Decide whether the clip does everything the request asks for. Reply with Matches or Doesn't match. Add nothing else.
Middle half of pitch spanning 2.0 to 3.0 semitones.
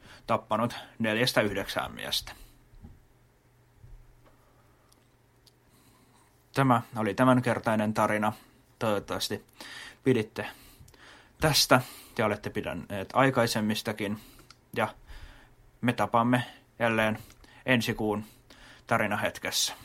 Matches